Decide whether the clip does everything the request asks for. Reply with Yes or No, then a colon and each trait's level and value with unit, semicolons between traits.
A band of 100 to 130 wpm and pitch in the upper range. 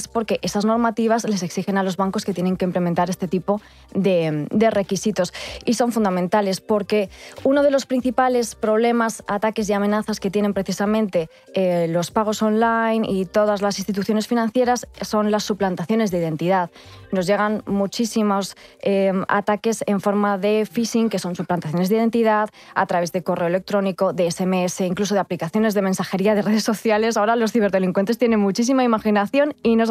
No: average, 165 wpm; high, 205 Hz